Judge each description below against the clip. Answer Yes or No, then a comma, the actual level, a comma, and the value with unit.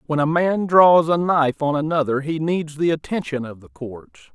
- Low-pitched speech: No, medium, 155 Hz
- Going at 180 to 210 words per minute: Yes, fast, 205 wpm